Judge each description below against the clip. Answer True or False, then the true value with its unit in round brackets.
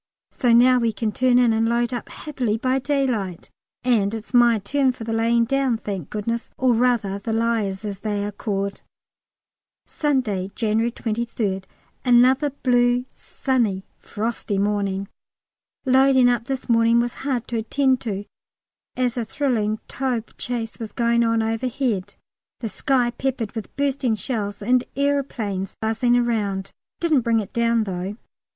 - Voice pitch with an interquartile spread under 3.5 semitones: True (3.0 semitones)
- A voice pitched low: False (235 Hz)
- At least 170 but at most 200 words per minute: False (150 wpm)